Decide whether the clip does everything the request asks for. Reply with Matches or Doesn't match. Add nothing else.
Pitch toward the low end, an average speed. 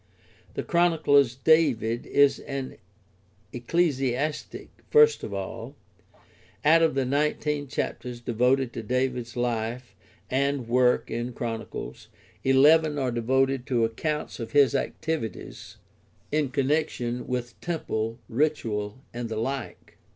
Doesn't match